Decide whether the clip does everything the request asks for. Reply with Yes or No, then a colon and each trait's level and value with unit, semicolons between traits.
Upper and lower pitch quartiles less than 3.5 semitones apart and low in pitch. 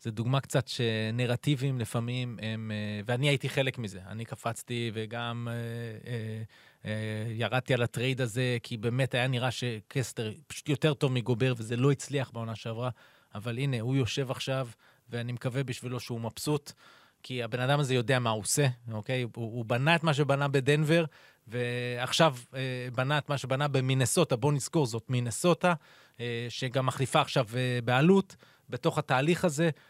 Yes: average, 2.9 semitones; low, 125 Hz